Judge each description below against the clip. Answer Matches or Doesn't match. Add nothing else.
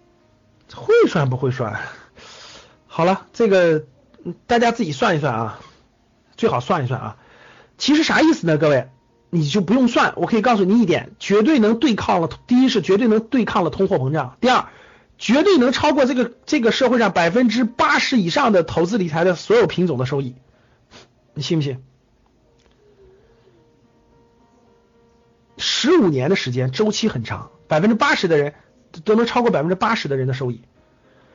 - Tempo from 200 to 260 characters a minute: Matches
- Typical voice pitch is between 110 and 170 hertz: Doesn't match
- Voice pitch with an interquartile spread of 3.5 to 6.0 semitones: Doesn't match